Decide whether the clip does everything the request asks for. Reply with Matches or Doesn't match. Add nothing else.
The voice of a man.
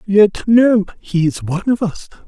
Matches